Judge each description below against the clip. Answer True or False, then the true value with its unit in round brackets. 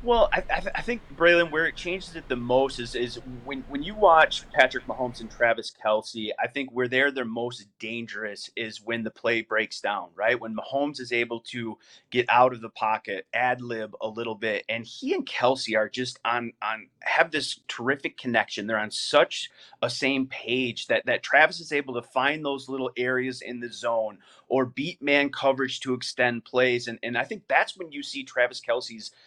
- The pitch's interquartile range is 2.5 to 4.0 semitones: True (2.9 semitones)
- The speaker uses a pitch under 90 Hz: False (125 Hz)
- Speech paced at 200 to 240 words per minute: True (205 wpm)